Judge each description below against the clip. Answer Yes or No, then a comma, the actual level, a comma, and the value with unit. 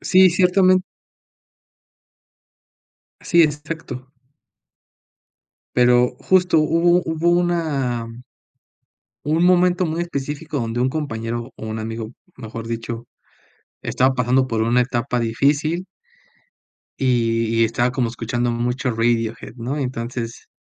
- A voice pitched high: No, low, 125 Hz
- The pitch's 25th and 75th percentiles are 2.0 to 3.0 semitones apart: No, wide, 5.6 semitones